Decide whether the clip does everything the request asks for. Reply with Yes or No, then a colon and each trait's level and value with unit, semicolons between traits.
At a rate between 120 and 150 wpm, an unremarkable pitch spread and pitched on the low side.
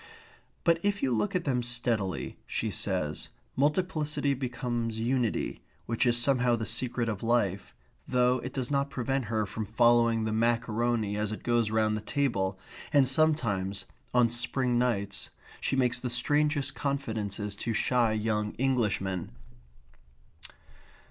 Yes: average, 140 wpm; average, 3.4 semitones; low, 120 Hz